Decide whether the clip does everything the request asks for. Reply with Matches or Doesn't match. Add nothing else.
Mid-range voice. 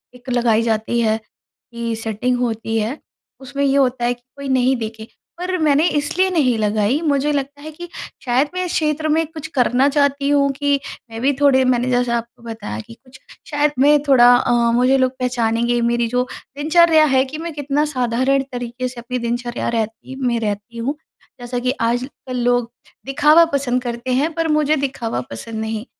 Doesn't match